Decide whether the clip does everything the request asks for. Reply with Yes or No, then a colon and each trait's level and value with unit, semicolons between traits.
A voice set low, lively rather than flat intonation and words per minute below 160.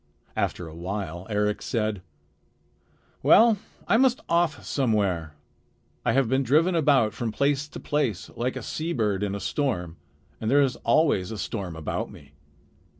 Yes: low, 115 Hz; wide, 6.7 semitones; average, 150 wpm